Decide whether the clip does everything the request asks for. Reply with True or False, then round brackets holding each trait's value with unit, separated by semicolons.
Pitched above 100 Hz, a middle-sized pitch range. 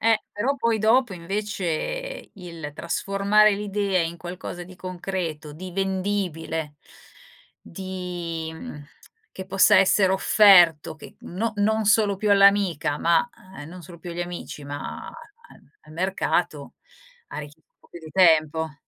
True (185 Hz; 3.6 semitones)